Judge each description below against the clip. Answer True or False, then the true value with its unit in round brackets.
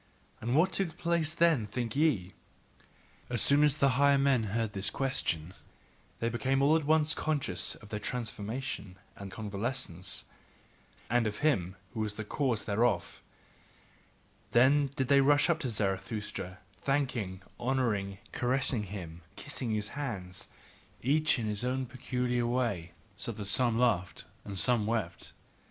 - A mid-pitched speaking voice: False (120 Hz)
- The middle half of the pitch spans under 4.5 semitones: False (5.1 semitones)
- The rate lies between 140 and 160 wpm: True (145 wpm)